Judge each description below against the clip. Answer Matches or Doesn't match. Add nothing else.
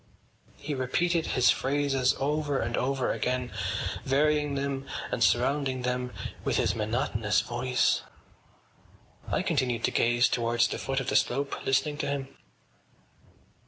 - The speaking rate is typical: Doesn't match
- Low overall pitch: Matches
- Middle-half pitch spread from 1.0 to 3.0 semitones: Matches